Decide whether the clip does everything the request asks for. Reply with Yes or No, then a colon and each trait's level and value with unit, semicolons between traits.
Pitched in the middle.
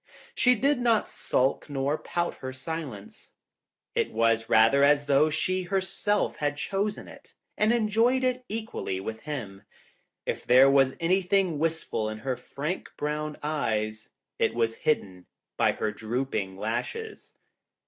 Yes: medium, 145 Hz